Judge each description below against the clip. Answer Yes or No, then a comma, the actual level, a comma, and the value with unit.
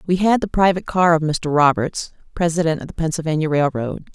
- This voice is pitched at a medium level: Yes, medium, 165 Hz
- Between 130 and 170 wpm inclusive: No, average, 190 wpm